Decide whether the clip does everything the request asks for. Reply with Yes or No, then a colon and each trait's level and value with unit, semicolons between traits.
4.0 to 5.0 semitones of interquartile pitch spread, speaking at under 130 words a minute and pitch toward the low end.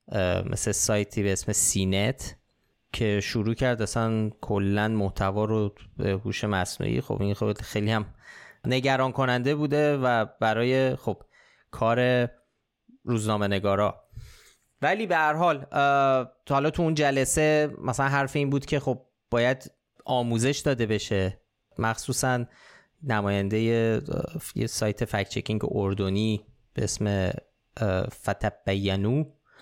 Yes: average, 4.3 semitones; average, 115 wpm; low, 115 Hz